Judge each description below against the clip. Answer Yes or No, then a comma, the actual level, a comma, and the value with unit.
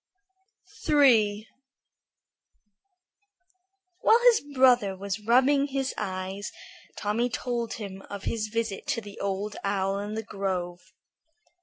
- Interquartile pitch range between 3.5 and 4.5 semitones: Yes, average, 3.9 semitones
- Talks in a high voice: Yes, high, 210 Hz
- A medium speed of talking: No, slow, 110 wpm